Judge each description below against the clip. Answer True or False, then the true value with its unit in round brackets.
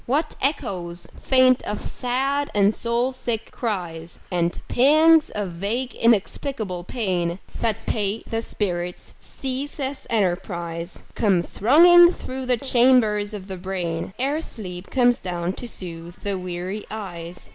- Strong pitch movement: True (6.2 semitones)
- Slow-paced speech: True (130 wpm)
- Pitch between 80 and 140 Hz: False (210 Hz)